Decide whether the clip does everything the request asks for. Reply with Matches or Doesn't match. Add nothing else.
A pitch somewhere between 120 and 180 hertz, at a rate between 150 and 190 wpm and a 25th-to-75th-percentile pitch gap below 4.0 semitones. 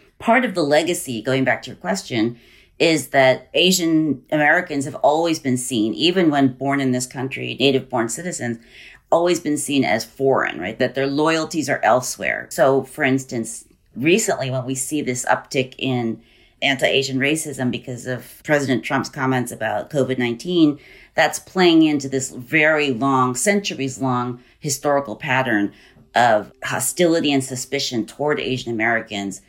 Matches